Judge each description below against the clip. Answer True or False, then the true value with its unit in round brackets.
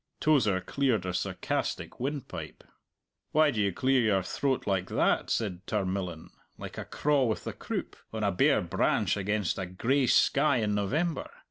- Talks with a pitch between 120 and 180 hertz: False (105 Hz)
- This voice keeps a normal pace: True (160 wpm)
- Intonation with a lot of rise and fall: True (6.0 semitones)